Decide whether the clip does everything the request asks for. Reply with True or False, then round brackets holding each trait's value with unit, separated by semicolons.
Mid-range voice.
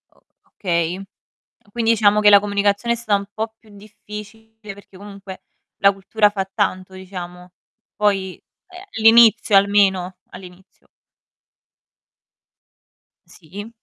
False (200 Hz)